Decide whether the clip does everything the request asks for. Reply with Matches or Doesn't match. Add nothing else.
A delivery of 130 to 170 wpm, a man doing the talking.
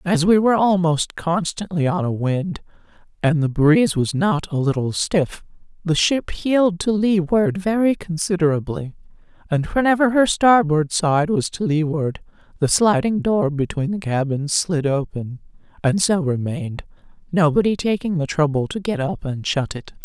Doesn't match